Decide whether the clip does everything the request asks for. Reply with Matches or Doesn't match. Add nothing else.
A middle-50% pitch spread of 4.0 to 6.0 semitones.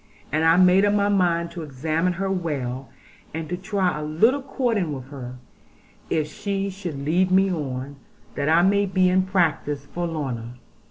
Matches